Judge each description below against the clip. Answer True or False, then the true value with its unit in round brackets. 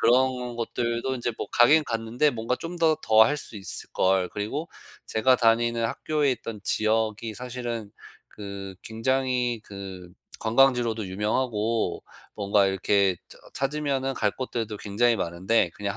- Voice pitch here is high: False (115 Hz)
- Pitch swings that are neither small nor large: True (3.5 semitones)